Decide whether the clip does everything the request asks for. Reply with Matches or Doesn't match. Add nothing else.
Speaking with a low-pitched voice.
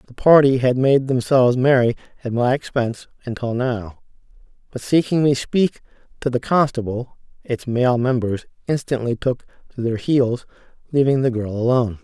Matches